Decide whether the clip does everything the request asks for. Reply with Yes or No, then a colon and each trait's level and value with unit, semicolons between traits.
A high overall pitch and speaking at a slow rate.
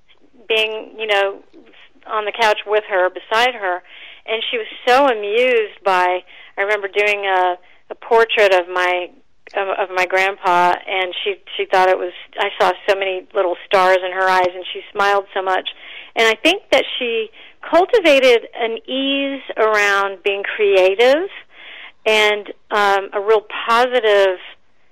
No: high, 205 Hz; average, 150 wpm